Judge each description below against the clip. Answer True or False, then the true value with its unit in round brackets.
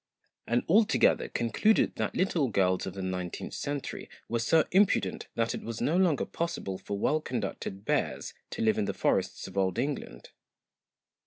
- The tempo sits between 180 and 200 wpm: False (170 wpm)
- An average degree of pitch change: False (8.3 semitones)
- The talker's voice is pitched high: False (115 Hz)